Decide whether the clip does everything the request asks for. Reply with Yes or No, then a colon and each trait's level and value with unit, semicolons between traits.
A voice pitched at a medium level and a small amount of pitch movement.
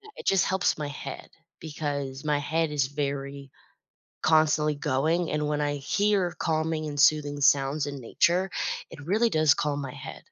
Yes: medium, 150 Hz; narrow, 2.0 semitones